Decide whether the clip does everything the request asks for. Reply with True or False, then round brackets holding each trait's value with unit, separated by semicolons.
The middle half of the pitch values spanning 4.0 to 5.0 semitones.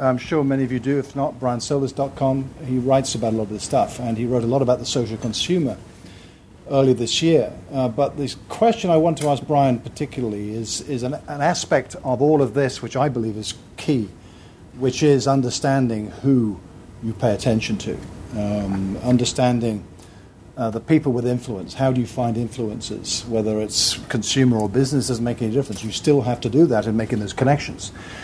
False (3.6 semitones)